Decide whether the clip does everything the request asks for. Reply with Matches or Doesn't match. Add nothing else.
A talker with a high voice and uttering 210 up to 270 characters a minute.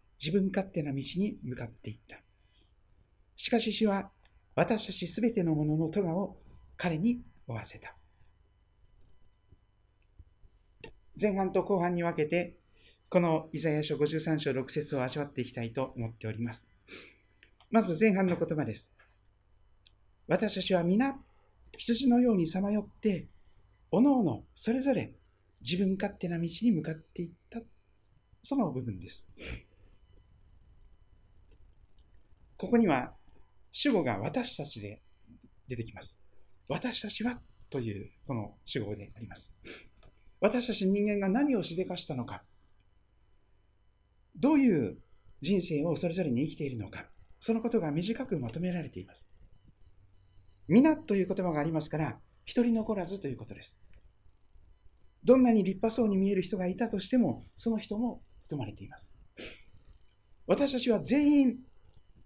Doesn't match